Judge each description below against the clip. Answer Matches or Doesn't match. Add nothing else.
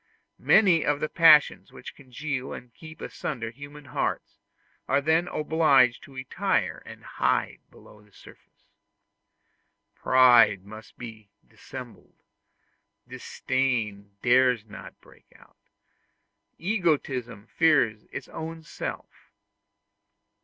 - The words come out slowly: Matches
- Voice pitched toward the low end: Matches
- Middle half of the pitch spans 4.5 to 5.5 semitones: Matches